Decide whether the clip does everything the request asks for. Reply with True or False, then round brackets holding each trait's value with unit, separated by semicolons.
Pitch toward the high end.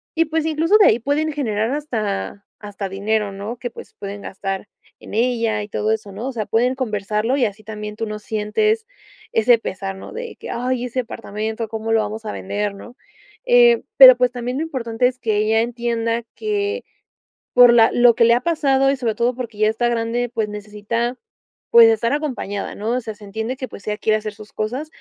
True (230 Hz)